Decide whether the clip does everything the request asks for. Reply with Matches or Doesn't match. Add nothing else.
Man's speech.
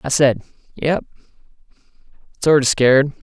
Matches